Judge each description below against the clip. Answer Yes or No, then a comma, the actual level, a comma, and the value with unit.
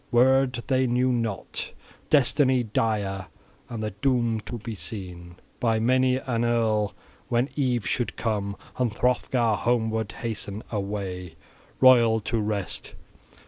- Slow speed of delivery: Yes, slow, 125 wpm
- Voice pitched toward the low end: Yes, low, 115 Hz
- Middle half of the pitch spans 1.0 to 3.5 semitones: Yes, average, 3.1 semitones